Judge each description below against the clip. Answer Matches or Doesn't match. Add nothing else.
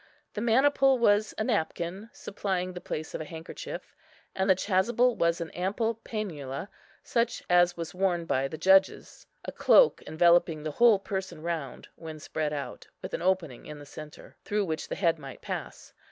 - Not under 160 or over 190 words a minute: Matches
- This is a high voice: Doesn't match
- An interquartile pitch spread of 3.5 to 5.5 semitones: Matches